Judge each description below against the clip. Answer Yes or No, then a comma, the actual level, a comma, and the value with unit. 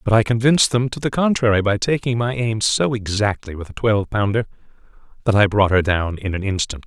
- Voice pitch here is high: No, low, 110 Hz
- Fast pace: Yes, fast, 220 wpm